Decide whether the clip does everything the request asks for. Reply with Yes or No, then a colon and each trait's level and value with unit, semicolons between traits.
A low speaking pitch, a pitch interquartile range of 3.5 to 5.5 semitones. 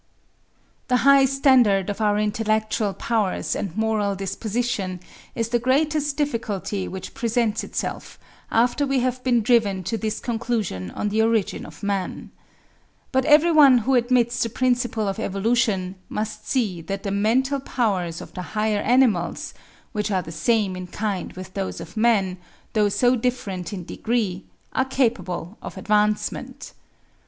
No: high, 220 Hz; average, 3.8 semitones